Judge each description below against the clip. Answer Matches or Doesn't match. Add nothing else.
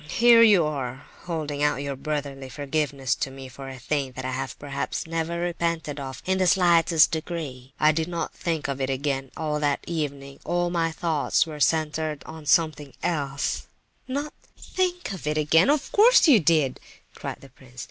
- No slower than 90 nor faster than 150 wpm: Doesn't match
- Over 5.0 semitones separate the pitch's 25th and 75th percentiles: Doesn't match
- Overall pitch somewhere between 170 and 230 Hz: Doesn't match